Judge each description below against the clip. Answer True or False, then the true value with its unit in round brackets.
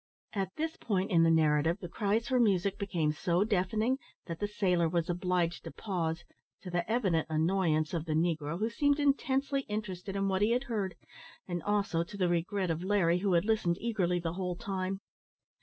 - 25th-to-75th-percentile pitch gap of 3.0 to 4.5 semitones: True (3.6 semitones)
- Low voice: False (185 Hz)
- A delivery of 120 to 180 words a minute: False (190 wpm)